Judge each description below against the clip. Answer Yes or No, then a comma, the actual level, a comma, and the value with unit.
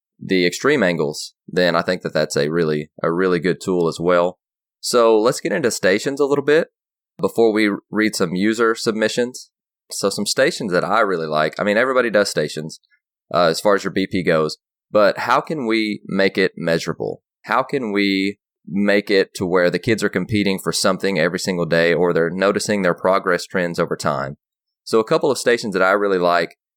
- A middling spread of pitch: Yes, average, 3.7 semitones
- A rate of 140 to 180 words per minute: No, average, 200 wpm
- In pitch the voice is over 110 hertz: No, very low, 95 Hz